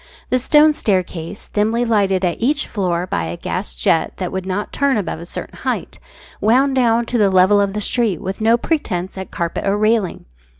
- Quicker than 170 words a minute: Yes, average, 200 wpm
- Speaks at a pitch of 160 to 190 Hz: No, high, 205 Hz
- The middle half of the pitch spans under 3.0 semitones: No, average, 4.2 semitones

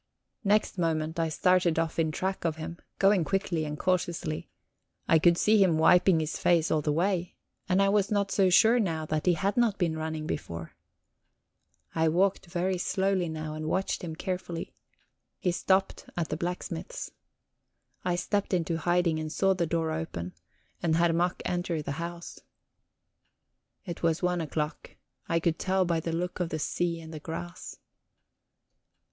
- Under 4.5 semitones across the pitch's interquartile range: Yes, narrow, 2.6 semitones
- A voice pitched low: No, medium, 170 Hz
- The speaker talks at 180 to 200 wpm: No, average, 170 wpm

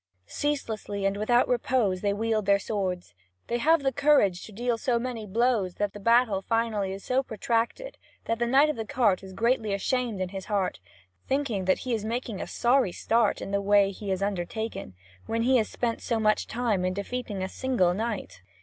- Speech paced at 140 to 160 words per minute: No, average, 200 wpm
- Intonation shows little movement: No, average, 3.6 semitones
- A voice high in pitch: Yes, high, 220 Hz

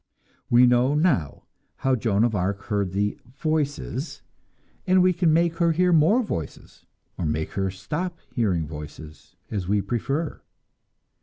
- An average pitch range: No, wide, 8.9 semitones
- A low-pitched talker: Yes, low, 120 Hz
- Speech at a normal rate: Yes, average, 145 wpm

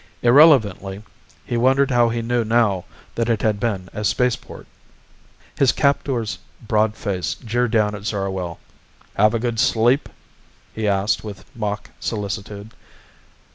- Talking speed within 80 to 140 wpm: Yes, slow, 135 wpm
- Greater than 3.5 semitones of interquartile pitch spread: No, average, 2.8 semitones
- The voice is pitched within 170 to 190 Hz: No, low, 110 Hz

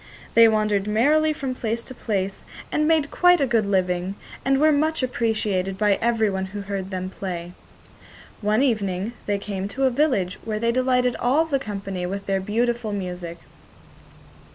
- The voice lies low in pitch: No, high, 215 Hz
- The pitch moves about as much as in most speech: Yes, average, 4.7 semitones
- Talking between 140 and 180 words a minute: Yes, average, 165 wpm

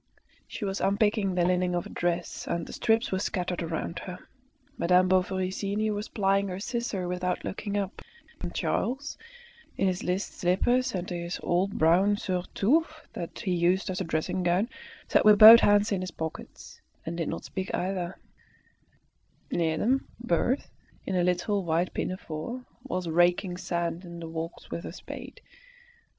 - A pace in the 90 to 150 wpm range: No, average, 165 wpm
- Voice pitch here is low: No, medium, 185 Hz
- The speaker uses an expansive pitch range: No, average, 2.7 semitones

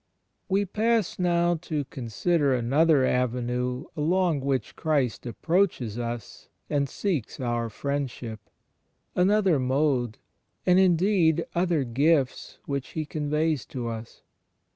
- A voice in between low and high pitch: Yes, medium, 145 Hz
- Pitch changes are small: No, wide, 5.4 semitones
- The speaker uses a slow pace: Yes, slow, 110 wpm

